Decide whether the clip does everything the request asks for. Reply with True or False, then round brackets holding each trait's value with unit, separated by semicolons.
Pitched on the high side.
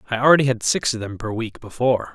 False (120 Hz)